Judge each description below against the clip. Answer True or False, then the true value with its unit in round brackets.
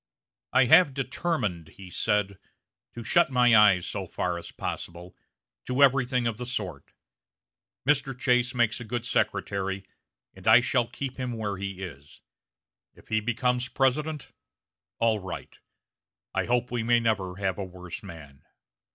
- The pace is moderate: True (150 wpm)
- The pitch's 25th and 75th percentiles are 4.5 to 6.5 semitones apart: True (4.8 semitones)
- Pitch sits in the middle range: False (115 Hz)